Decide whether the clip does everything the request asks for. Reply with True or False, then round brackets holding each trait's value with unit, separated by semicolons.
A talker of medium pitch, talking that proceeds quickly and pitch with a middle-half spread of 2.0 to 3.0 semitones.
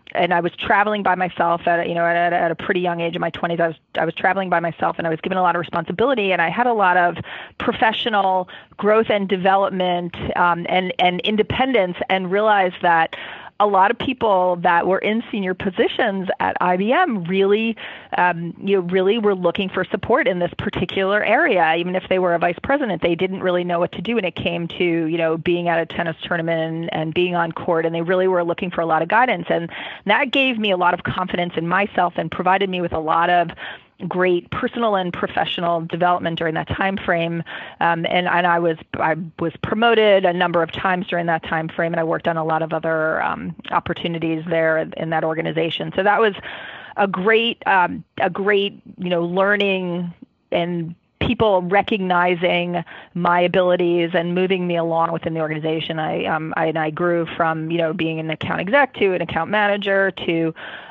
True (175 Hz; 210 wpm; 2.5 semitones)